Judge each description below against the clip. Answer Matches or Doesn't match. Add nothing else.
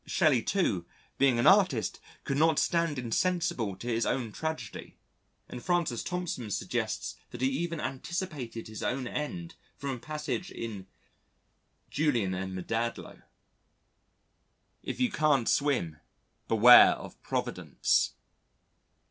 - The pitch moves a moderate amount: Doesn't match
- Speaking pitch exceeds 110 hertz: Matches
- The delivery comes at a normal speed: Doesn't match